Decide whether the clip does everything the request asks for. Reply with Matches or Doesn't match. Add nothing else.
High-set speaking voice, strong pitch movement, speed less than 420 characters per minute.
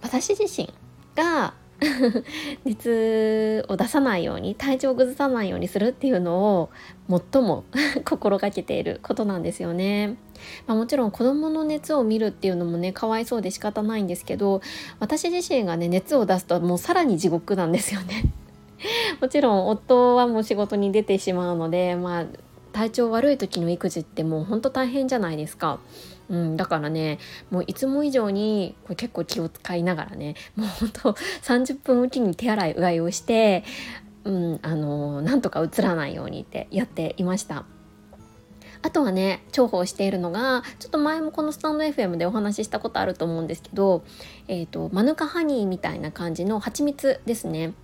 Matches